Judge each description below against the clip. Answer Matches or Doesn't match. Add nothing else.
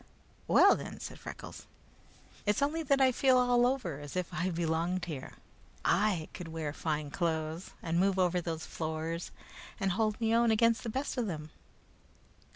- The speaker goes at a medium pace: Matches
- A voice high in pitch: Doesn't match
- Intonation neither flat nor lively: Doesn't match